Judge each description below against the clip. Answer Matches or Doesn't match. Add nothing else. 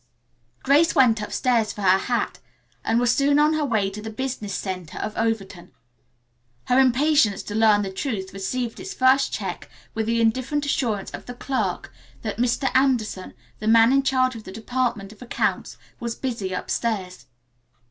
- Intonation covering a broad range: Doesn't match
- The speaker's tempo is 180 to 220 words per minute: Doesn't match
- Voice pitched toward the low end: Doesn't match